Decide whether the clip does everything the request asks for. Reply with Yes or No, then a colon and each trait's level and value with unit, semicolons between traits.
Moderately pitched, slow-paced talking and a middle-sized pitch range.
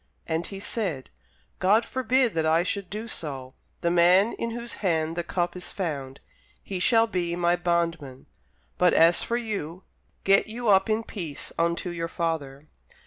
No: medium, 175 Hz; average, 165 wpm; average, 4.1 semitones